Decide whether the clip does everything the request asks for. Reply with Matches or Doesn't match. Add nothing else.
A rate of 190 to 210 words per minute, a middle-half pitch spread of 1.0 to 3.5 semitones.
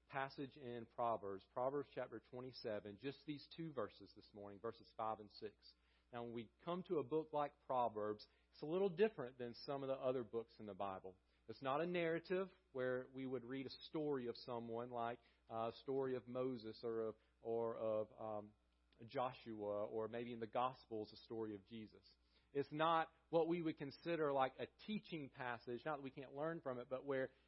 Doesn't match